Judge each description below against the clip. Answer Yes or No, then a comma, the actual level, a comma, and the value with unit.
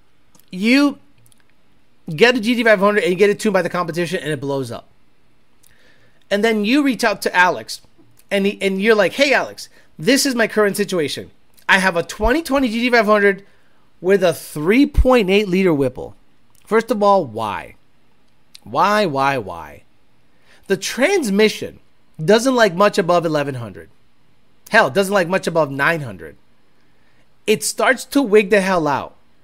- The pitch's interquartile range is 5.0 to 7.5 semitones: Yes, wide, 5.4 semitones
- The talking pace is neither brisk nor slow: Yes, average, 145 wpm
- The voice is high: Yes, high, 200 Hz